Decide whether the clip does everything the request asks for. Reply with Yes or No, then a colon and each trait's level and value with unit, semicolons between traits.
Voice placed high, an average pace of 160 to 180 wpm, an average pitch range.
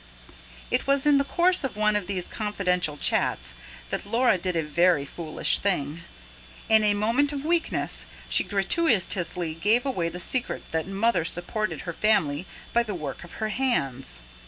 No: high, 200 Hz; average, 165 wpm; wide, 5.8 semitones